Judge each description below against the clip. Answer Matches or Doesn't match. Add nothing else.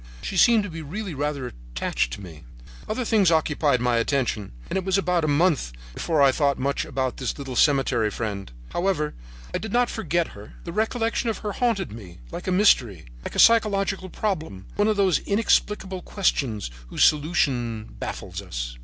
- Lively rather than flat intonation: Matches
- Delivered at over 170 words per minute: Matches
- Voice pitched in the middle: Matches